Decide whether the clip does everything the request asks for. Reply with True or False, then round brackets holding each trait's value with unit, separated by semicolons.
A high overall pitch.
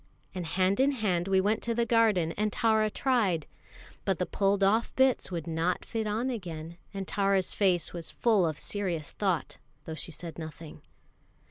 True (195 Hz)